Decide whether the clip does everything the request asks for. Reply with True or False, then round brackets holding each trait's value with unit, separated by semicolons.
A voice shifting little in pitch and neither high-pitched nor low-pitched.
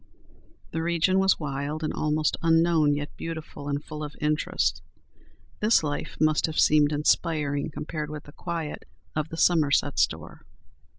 True (1.7 semitones; 155 Hz)